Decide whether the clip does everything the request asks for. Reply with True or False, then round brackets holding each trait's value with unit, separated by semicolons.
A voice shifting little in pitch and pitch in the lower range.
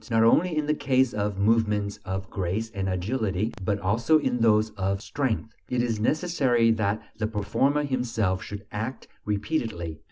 False (3.6 semitones; 110 Hz)